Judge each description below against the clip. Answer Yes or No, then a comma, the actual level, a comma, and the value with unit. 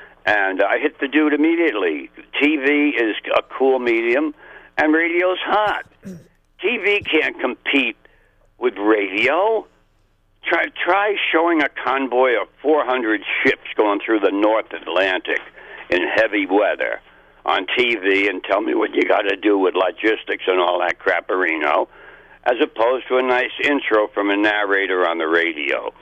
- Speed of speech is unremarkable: Yes, average, 145 wpm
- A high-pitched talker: No, medium, 140 Hz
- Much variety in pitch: Yes, wide, 8.6 semitones